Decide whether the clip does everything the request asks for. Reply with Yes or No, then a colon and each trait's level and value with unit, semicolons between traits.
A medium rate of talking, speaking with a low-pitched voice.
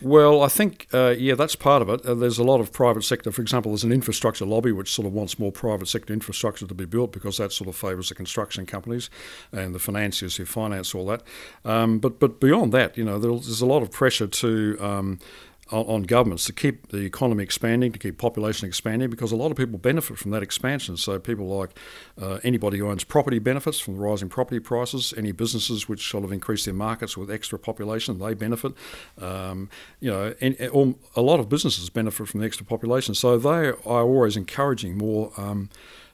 No: fast, 220 wpm; low, 110 Hz